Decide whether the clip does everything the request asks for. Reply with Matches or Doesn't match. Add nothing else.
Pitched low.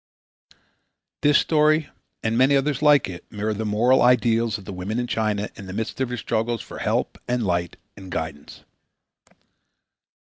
Matches